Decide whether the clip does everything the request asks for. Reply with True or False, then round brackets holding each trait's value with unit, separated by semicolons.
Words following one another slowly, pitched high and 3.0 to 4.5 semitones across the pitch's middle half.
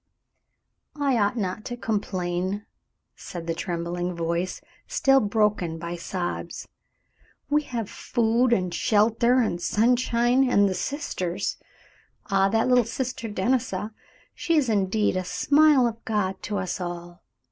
False (130 wpm; 210 Hz; 4.9 semitones)